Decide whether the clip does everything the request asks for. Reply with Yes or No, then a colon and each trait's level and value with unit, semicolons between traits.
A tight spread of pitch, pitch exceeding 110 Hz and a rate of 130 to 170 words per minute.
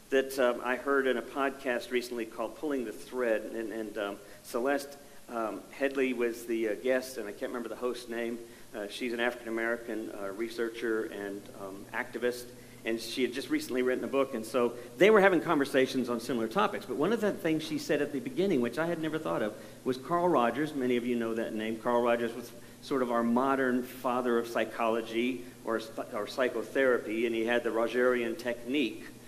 No: narrow, 2.1 semitones; low, 120 Hz; fast, 205 wpm